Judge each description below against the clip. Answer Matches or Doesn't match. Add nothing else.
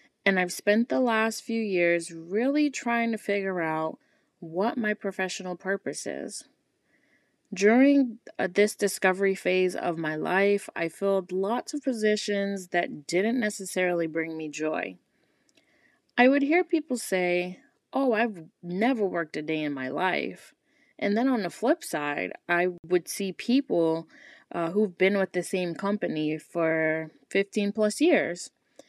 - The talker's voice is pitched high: Matches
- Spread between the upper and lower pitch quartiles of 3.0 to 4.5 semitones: Doesn't match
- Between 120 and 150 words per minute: Matches